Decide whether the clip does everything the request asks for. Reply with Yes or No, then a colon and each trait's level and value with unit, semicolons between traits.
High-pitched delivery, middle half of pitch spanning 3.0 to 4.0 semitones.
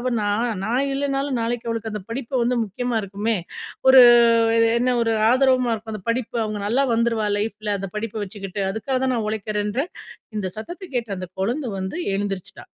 Yes: high, 230 Hz; average, 3.4 semitones